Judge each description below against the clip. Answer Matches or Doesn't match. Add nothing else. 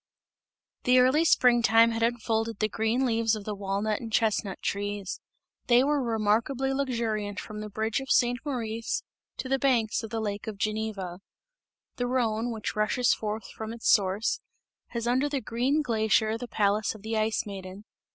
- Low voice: Doesn't match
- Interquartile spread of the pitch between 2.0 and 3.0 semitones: Matches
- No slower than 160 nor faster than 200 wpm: Matches